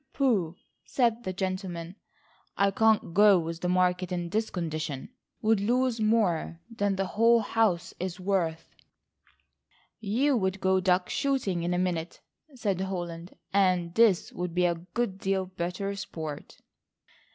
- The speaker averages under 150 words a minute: Yes, average, 140 wpm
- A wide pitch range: No, average, 3.4 semitones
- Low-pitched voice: No, high, 190 Hz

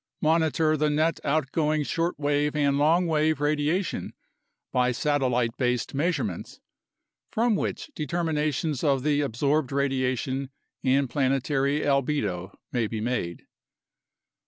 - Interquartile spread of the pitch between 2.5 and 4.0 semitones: Yes, average, 3.0 semitones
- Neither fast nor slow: No, slow, 110 wpm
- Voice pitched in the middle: Yes, medium, 145 Hz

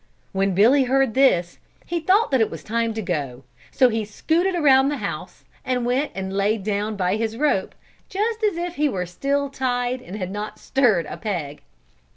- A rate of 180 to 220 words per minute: Yes, average, 190 wpm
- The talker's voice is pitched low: No, high, 230 Hz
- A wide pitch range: Yes, wide, 6.1 semitones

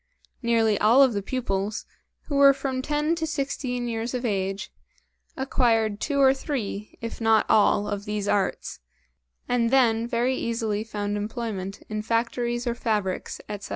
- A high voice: Yes, high, 230 Hz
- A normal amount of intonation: Yes, average, 3.6 semitones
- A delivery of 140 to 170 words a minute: Yes, average, 155 wpm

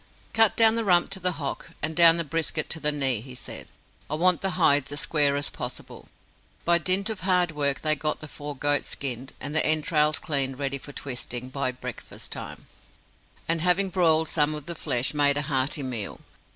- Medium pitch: Yes, medium, 150 Hz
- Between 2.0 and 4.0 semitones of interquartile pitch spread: Yes, average, 3.5 semitones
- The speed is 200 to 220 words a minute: Yes, fast, 205 wpm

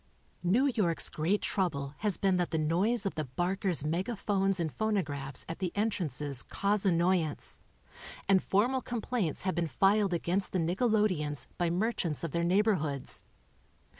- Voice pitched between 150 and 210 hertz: Yes, medium, 185 Hz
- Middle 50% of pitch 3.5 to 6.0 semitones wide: Yes, average, 4.1 semitones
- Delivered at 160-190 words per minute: No, average, 150 wpm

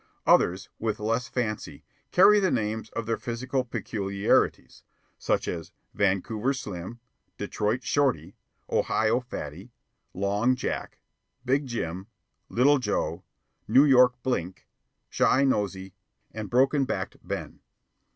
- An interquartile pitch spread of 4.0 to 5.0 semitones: Yes, average, 4.4 semitones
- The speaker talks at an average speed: No, slow, 110 wpm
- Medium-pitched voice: No, low, 115 Hz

